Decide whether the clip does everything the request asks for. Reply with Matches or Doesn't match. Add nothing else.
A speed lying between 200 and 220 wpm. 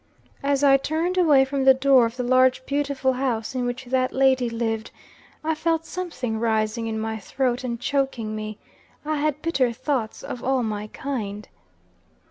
Doesn't match